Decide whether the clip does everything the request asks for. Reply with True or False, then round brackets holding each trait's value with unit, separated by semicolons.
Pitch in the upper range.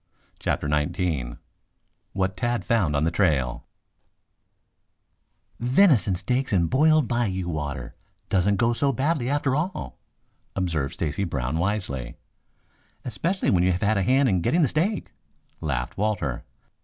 False (95 Hz)